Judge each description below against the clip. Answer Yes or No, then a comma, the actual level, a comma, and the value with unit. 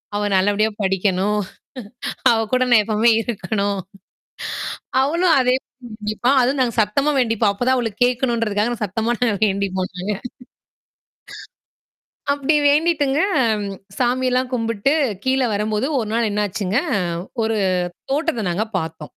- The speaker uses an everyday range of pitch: Yes, average, 3.7 semitones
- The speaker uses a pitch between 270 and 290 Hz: No, high, 225 Hz